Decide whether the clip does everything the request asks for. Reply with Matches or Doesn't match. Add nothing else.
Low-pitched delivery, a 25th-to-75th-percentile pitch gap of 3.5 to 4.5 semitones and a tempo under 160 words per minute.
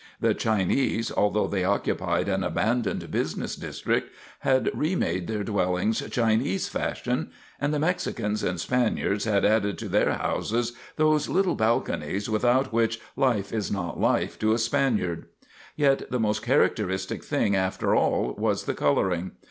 Matches